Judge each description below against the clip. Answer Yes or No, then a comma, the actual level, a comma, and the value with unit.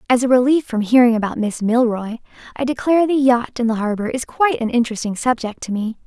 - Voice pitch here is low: No, high, 240 Hz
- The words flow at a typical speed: No, fast, 220 wpm